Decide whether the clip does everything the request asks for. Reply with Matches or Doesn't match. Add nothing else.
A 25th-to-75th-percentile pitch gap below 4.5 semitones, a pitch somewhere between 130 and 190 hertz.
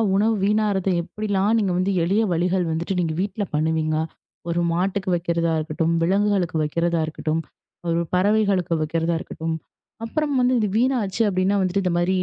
Matches